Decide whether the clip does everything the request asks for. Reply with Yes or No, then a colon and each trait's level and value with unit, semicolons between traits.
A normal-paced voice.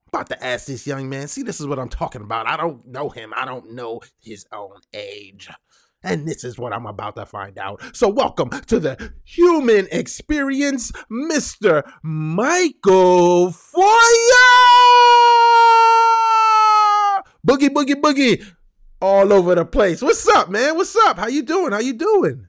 Yes: average, 155 wpm